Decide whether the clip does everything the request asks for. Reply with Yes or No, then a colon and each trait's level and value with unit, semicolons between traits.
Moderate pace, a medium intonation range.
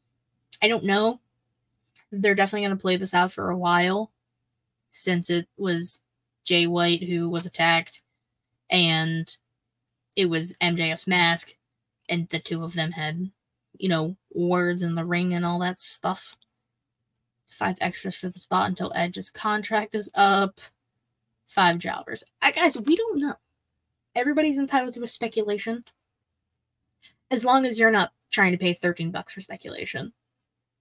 No: average, 150 wpm; wide, 8.1 semitones